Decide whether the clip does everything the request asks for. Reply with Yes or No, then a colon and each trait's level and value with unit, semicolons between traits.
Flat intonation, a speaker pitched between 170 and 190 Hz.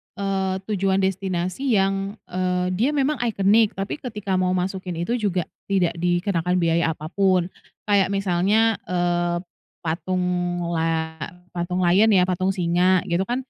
Yes: narrow, 2.0 semitones; medium, 185 Hz